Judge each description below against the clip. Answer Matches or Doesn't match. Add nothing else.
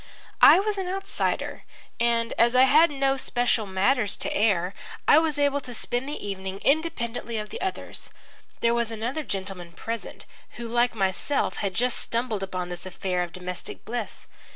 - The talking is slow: Doesn't match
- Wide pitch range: Matches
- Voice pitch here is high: Matches